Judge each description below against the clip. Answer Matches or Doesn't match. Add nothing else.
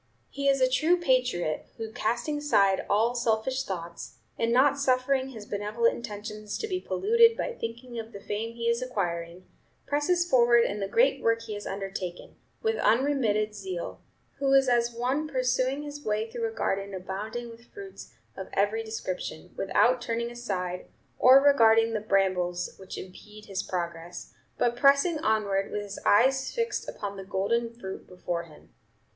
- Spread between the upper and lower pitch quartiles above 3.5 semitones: Matches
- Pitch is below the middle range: Doesn't match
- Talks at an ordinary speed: Matches